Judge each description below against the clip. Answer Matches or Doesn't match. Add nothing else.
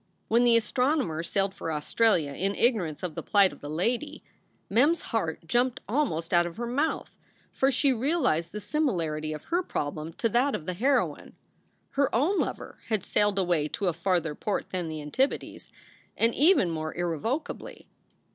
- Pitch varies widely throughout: Matches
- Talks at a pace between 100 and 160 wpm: Doesn't match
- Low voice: Doesn't match